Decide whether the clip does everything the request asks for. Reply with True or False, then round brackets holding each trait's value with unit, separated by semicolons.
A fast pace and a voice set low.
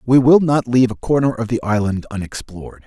True (210 wpm; 115 Hz)